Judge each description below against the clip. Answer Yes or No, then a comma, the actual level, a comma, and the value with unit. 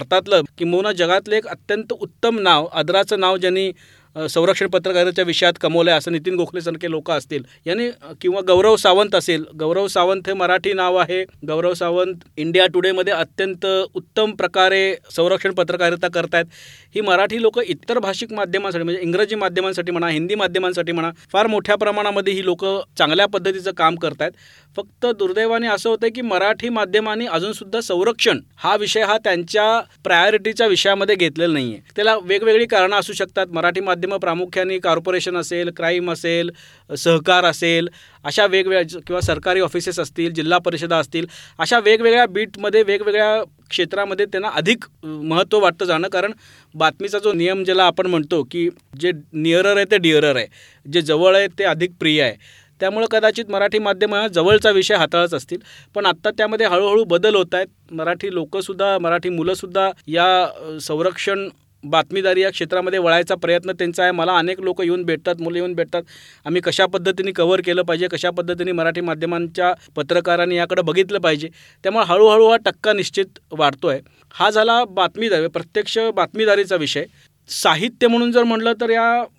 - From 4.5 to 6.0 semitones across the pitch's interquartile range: No, average, 3.0 semitones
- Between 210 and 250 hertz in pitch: No, medium, 185 Hz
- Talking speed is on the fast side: Yes, fast, 155 wpm